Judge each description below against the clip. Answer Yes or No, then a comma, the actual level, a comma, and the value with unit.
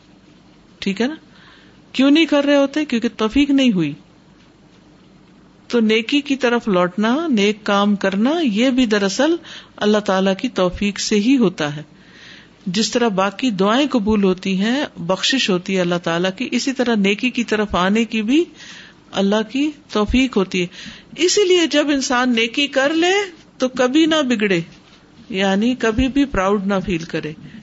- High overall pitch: Yes, high, 225 Hz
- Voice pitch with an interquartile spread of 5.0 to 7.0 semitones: Yes, wide, 5.6 semitones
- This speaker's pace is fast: No, average, 160 wpm